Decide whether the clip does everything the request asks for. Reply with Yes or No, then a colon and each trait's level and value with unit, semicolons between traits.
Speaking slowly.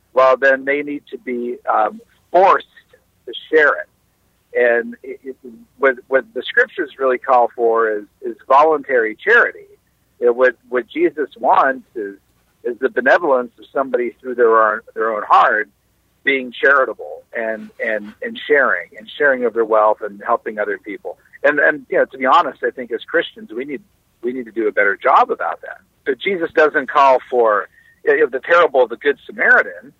No: average, 185 wpm